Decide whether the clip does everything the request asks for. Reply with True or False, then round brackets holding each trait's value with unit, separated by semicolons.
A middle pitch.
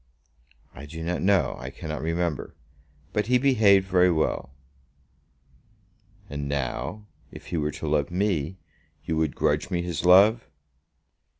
False (85 Hz)